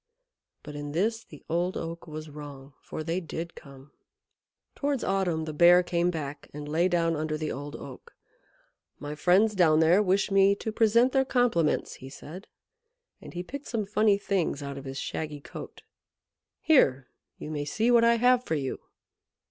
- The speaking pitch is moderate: Yes, medium, 170 Hz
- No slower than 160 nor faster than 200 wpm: Yes, average, 175 wpm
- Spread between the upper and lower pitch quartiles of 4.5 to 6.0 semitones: Yes, average, 5.3 semitones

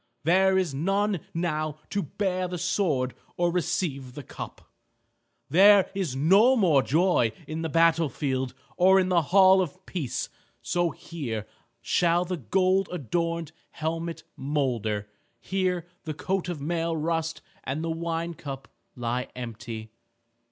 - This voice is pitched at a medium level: Yes, medium, 165 Hz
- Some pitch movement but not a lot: Yes, average, 4.6 semitones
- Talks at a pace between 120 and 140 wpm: Yes, slow, 135 wpm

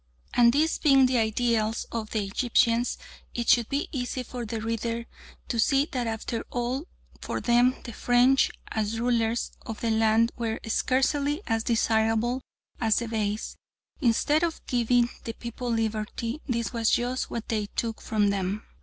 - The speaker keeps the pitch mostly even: Yes, narrow, 1.9 semitones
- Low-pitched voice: No, high, 235 Hz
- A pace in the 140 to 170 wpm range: Yes, average, 160 wpm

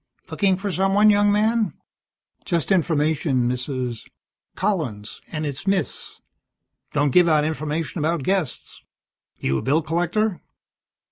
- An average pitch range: Yes, average, 4.9 semitones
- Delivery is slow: Yes, slow, 125 wpm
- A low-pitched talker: No, medium, 165 Hz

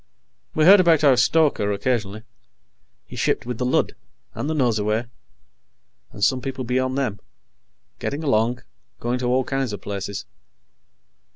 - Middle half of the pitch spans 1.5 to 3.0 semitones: No, average, 3.9 semitones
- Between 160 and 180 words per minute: No, average, 145 wpm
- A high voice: No, low, 125 Hz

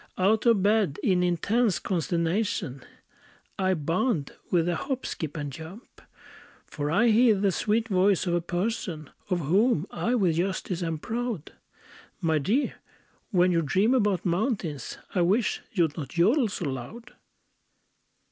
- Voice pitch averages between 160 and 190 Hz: Yes, medium, 185 Hz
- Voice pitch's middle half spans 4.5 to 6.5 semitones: Yes, average, 4.9 semitones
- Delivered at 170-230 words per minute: No, average, 145 wpm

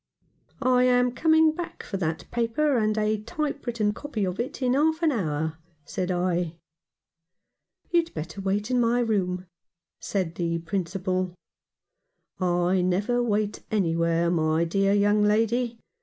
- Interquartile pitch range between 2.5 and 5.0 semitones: No, wide, 5.6 semitones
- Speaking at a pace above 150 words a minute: No, average, 145 wpm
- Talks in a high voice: Yes, high, 205 Hz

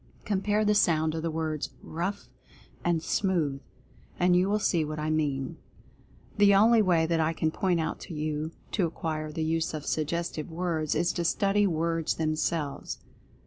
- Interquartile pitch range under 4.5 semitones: Yes, average, 2.7 semitones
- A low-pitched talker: No, medium, 165 Hz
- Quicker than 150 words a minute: Yes, average, 170 wpm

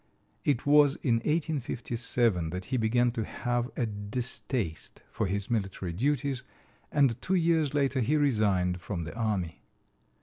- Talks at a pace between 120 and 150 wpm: Yes, average, 140 wpm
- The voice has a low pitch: Yes, low, 120 Hz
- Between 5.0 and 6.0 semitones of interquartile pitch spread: Yes, wide, 5.5 semitones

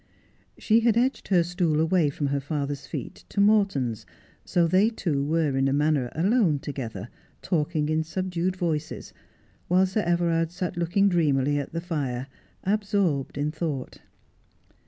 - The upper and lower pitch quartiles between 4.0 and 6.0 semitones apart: Yes, average, 4.4 semitones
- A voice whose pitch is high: No, medium, 165 Hz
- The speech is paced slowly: No, average, 150 wpm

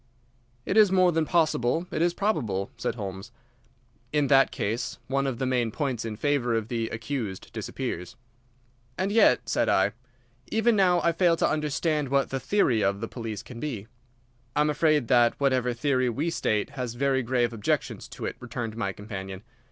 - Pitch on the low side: Yes, low, 130 Hz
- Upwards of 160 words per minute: Yes, average, 180 wpm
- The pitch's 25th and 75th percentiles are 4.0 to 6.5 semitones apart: Yes, average, 5.1 semitones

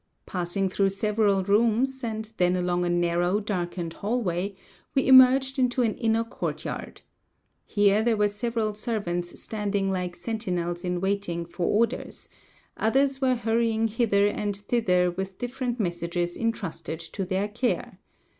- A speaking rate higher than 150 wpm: No, slow, 135 wpm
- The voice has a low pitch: No, high, 205 Hz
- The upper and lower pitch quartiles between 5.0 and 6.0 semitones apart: No, average, 4.2 semitones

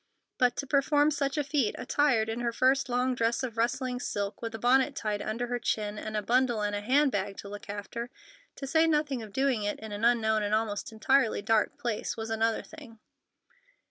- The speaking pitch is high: Yes, high, 235 Hz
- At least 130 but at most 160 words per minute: No, average, 200 wpm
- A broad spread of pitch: No, average, 3.7 semitones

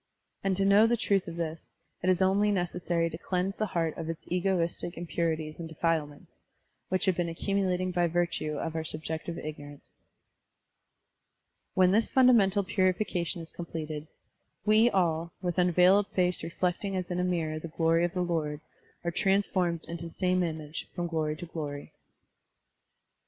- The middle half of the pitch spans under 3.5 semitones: Yes, narrow, 2.5 semitones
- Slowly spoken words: No, average, 160 wpm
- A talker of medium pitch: Yes, medium, 175 Hz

